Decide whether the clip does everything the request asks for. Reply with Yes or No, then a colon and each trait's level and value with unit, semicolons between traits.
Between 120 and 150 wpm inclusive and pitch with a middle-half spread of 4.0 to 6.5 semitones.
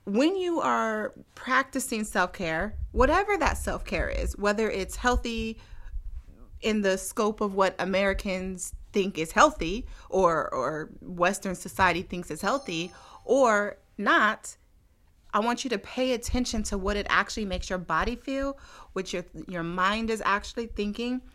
Yes: average, 145 wpm; average, 4.4 semitones